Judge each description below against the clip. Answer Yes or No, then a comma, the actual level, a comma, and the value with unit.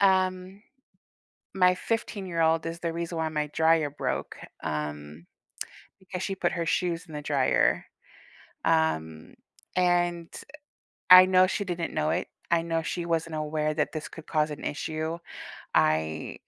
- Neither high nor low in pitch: Yes, medium, 165 Hz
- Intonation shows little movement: No, average, 3.3 semitones